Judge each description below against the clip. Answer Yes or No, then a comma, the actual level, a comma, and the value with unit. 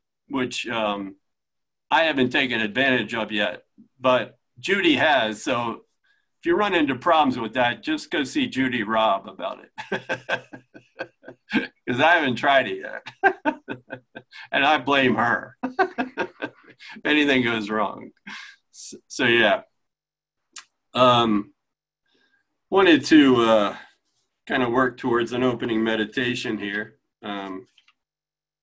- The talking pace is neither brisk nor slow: No, slow, 115 wpm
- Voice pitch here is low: Yes, low, 130 Hz